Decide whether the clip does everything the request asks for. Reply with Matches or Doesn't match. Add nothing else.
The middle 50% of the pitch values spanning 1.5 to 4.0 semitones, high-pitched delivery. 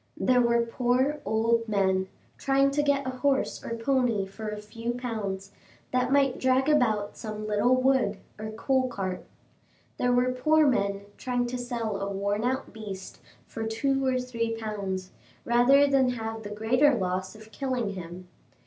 Matches